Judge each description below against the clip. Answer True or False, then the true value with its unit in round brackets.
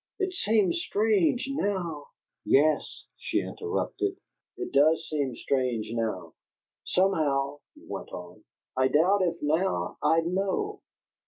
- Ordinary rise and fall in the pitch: False (6.7 semitones)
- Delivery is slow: True (120 wpm)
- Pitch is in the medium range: True (165 Hz)